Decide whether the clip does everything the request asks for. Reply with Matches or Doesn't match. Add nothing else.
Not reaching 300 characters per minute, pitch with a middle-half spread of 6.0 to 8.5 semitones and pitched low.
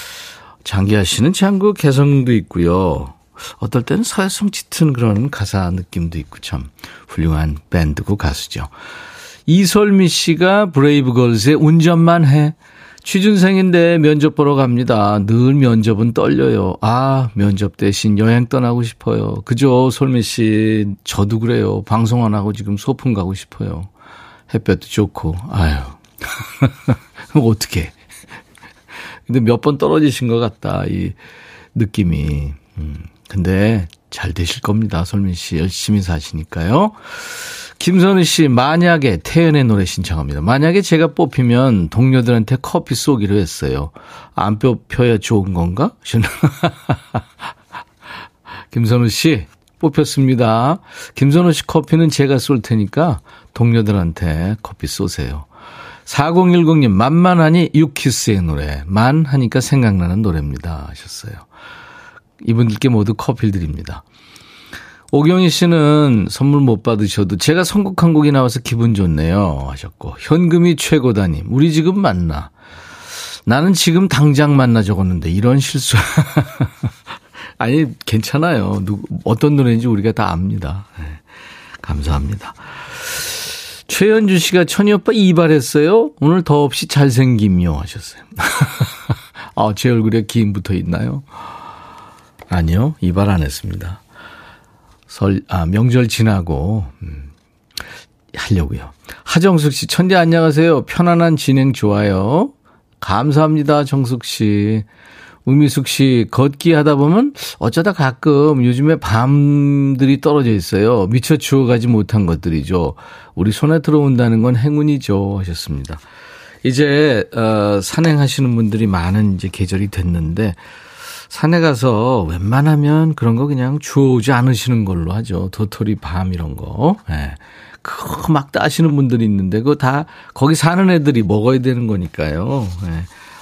Matches